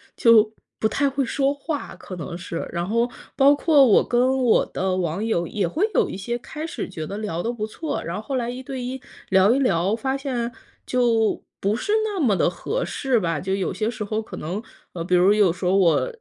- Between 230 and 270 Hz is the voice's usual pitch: No, high, 220 Hz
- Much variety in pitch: Yes, wide, 5.8 semitones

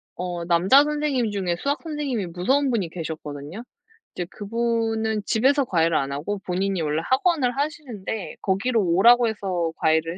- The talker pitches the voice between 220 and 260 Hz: No, high, 205 Hz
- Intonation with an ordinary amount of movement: No, wide, 6.6 semitones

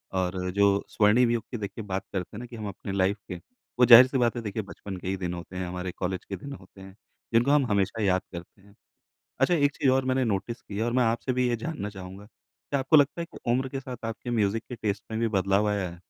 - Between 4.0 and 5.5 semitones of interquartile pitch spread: Yes, average, 4.4 semitones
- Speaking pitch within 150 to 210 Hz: No, low, 110 Hz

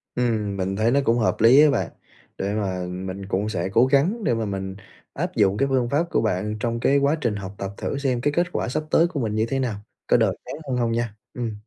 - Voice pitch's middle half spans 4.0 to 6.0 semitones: Yes, average, 5.1 semitones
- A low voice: Yes, low, 115 Hz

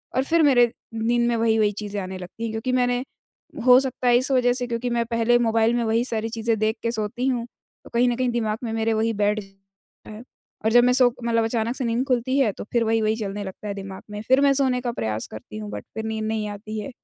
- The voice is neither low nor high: No, high, 230 Hz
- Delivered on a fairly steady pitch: Yes, narrow, 2.2 semitones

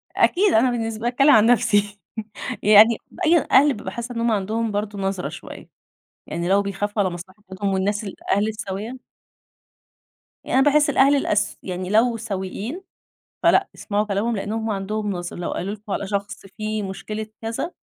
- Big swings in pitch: No, average, 2.8 semitones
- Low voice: No, high, 210 Hz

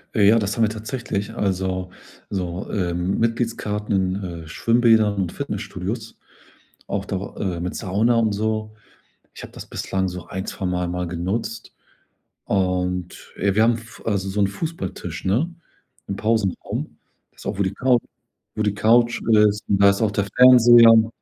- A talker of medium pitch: No, low, 100 Hz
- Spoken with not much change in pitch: No, average, 3.2 semitones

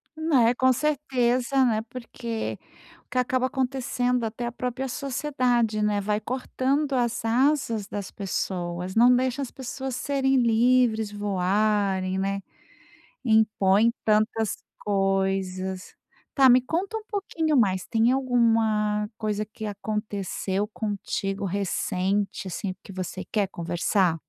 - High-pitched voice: Yes, high, 225 Hz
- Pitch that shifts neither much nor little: Yes, average, 4.2 semitones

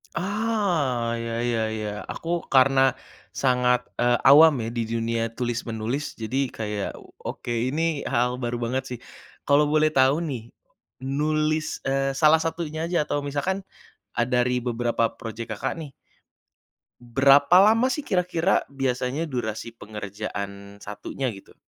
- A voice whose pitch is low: Yes, low, 130 Hz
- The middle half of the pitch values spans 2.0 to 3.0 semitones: No, average, 4.8 semitones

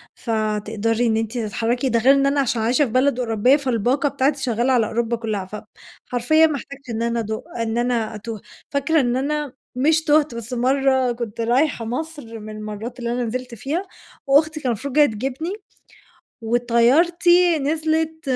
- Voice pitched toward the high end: Yes, very high, 250 Hz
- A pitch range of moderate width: Yes, average, 3.8 semitones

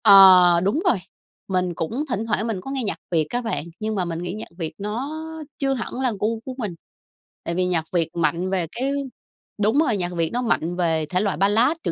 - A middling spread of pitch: Yes, average, 4.9 semitones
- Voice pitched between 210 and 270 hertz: No, high, 195 Hz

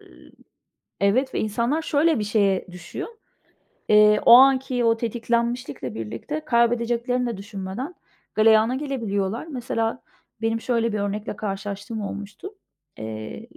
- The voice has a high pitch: Yes, high, 225 Hz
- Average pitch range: Yes, average, 3.5 semitones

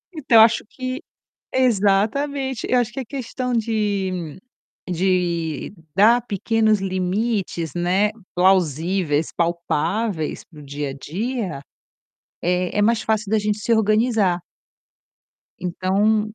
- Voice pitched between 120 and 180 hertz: No, high, 205 Hz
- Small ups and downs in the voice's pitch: No, average, 4.2 semitones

